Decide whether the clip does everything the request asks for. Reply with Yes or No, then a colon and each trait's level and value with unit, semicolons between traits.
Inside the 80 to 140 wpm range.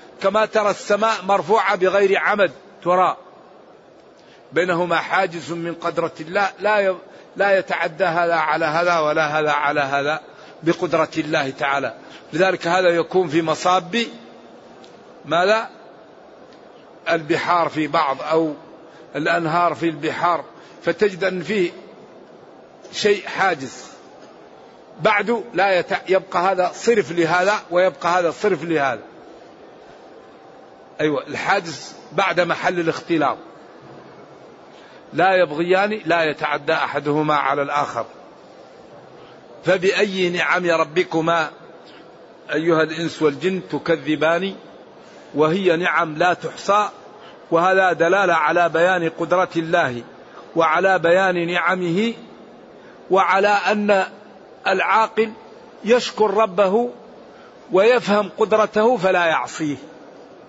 Yes: average, 95 wpm